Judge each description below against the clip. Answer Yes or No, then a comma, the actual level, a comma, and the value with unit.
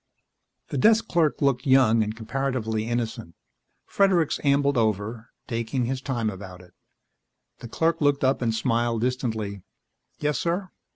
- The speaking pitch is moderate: No, low, 120 Hz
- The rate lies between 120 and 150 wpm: Yes, slow, 135 wpm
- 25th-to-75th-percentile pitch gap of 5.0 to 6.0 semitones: No, average, 4.1 semitones